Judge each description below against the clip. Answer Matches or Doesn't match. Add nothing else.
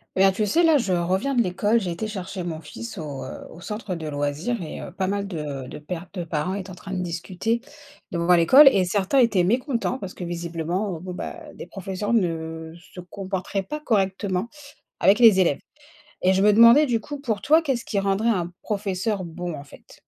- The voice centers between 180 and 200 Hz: Matches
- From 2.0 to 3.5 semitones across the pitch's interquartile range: Doesn't match